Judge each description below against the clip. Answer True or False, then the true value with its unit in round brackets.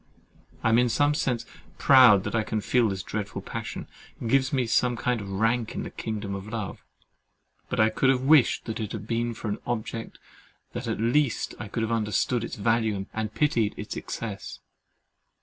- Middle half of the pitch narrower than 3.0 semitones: True (2.4 semitones)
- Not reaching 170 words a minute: False (180 wpm)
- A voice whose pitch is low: True (115 Hz)